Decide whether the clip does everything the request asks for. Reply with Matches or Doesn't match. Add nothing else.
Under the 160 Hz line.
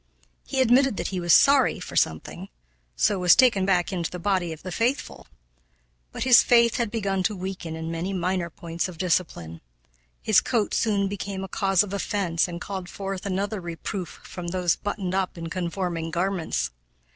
Doesn't match